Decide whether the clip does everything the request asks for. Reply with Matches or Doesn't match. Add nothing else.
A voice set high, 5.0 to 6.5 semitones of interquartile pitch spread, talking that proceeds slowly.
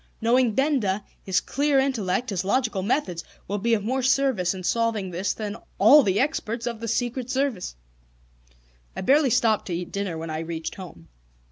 Doesn't match